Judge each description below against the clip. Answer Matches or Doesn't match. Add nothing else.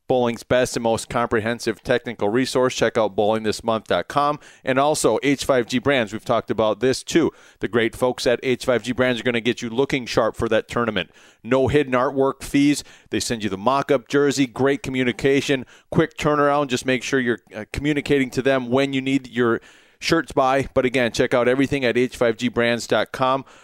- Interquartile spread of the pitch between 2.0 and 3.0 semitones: Matches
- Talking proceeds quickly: Doesn't match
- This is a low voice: Matches